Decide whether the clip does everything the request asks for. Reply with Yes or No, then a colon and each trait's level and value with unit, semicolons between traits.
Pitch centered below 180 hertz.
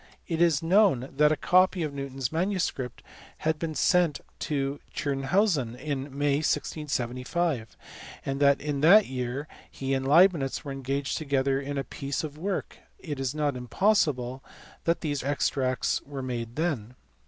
Yes: medium, 140 Hz